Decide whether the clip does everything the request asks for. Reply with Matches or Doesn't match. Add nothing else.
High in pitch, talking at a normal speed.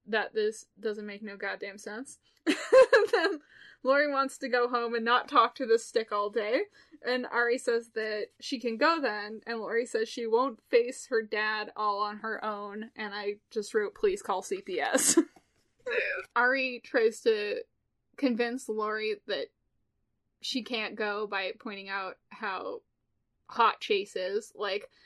Matches